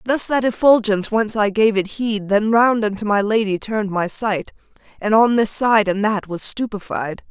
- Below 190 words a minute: No, average, 195 wpm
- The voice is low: No, high, 215 Hz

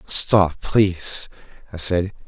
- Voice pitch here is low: Yes, very low, 90 Hz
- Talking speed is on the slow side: Yes, slow, 105 wpm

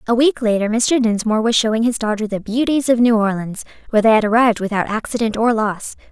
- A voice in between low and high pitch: No, high, 225 Hz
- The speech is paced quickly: Yes, fast, 215 wpm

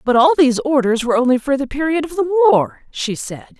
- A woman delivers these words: Yes, female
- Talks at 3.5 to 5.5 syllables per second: No, 6.1 syllables/s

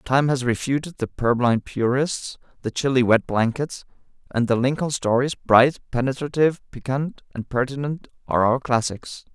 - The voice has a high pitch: No, low, 130 Hz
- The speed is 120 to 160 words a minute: Yes, average, 140 wpm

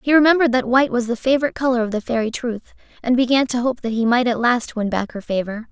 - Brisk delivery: Yes, fast, 260 wpm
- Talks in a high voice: Yes, high, 240 Hz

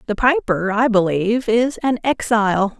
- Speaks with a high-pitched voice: Yes, high, 220 Hz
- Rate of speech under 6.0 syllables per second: Yes, 4.7 syllables/s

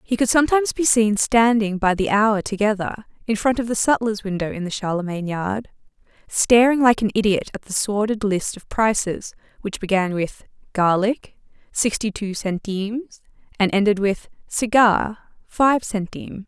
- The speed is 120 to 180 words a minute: Yes, average, 155 wpm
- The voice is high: Yes, high, 210 Hz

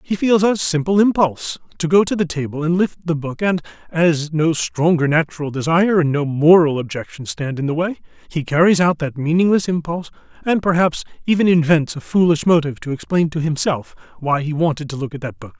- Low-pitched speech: No, medium, 160 Hz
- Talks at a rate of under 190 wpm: No, fast, 205 wpm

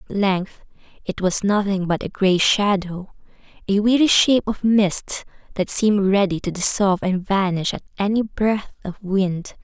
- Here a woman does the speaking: Yes, female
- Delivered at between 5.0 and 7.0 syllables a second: No, 4.6 syllables/s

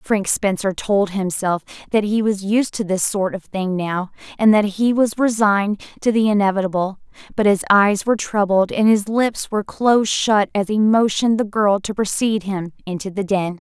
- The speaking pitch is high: Yes, high, 205 Hz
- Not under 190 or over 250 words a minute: Yes, average, 195 wpm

